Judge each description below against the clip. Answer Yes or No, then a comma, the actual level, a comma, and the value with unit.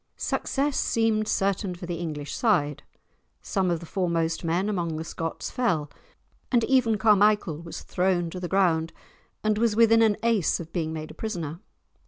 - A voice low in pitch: No, medium, 185 Hz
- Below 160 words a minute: No, average, 170 wpm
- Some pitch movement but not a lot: Yes, average, 4.7 semitones